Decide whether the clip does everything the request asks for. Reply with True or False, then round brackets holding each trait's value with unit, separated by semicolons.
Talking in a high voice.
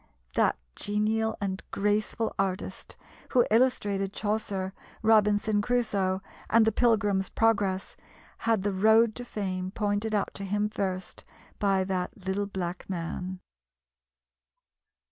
True (205 Hz)